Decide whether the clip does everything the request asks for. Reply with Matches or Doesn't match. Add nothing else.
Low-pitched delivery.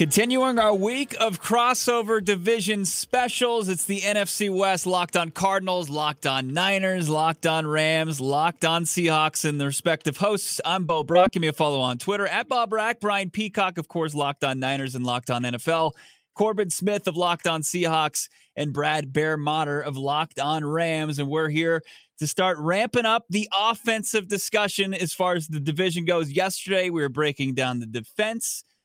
Doesn't match